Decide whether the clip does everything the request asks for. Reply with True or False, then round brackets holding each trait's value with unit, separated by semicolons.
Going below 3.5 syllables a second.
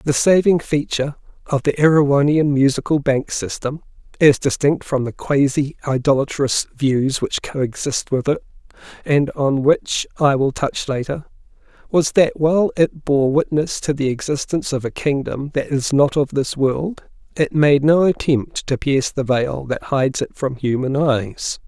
True (3.3 syllables/s)